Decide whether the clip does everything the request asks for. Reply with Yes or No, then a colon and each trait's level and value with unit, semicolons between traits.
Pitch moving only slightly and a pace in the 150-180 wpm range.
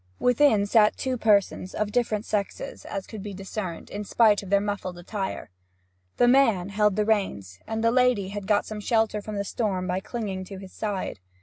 No: narrow, 2.3 semitones; fast, 205 wpm